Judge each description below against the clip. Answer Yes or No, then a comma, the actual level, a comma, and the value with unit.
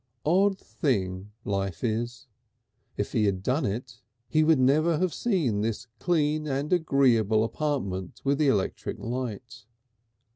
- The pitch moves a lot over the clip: Yes, wide, 6.3 semitones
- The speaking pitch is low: Yes, low, 130 Hz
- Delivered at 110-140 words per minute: Yes, slow, 135 wpm